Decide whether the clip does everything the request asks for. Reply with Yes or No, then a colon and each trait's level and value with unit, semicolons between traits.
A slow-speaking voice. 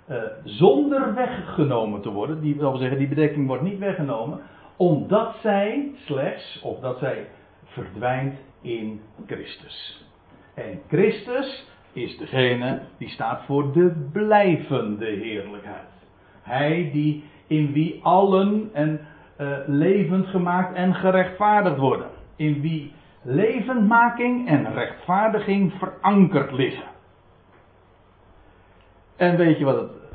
Yes: slow, 115 wpm